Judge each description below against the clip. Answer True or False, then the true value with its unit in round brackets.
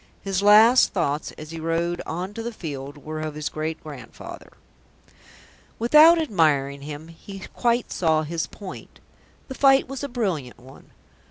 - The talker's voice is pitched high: False (165 Hz)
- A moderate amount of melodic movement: False (6.8 semitones)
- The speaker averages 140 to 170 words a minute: True (155 wpm)